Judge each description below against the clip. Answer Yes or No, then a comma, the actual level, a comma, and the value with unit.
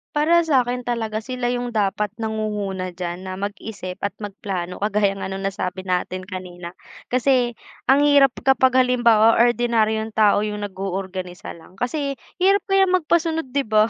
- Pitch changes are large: No, average, 4.7 semitones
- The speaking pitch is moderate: No, high, 220 Hz